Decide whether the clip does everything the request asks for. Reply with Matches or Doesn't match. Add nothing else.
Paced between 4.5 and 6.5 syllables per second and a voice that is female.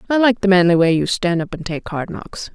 Matches